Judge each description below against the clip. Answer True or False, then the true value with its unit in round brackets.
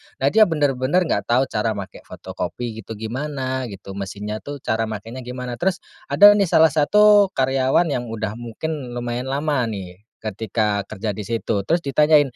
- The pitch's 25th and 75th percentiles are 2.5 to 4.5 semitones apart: False (5.1 semitones)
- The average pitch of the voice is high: False (125 Hz)